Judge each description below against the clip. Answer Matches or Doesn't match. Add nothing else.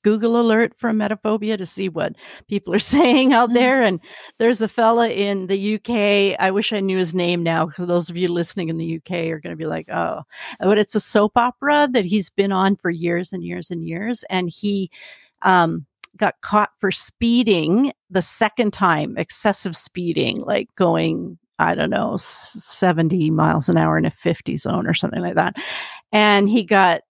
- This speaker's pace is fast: Doesn't match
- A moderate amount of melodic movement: Matches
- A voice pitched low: Doesn't match